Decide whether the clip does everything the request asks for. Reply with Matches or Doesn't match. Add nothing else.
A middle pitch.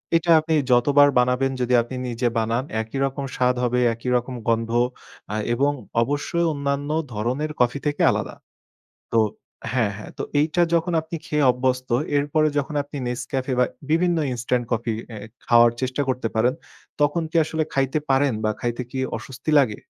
Doesn't match